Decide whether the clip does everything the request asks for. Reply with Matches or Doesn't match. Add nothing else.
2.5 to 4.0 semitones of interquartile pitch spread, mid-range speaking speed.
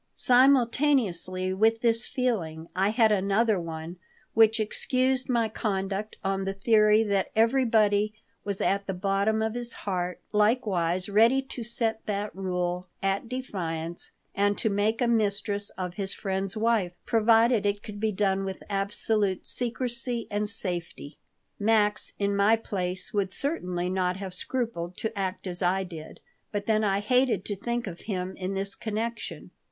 Matches